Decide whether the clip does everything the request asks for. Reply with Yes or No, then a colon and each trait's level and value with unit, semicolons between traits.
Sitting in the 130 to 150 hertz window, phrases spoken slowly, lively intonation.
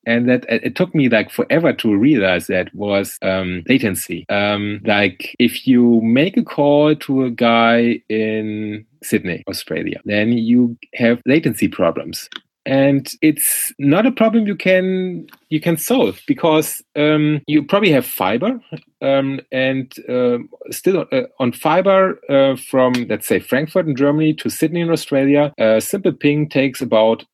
No: medium, 140 Hz; average, 155 wpm; wide, 6.3 semitones